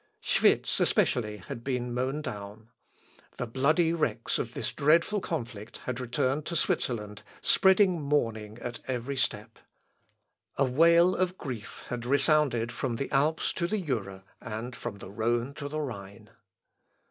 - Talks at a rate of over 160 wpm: No, average, 145 wpm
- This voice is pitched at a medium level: No, low, 130 Hz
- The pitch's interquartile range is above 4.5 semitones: Yes, average, 5.0 semitones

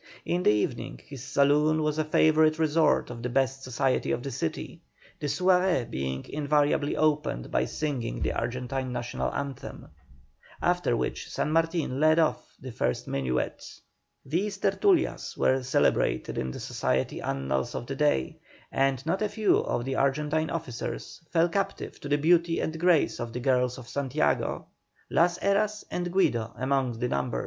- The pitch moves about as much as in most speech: Yes, average, 4.7 semitones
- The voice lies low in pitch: No, medium, 145 Hz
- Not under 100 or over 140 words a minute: No, average, 160 wpm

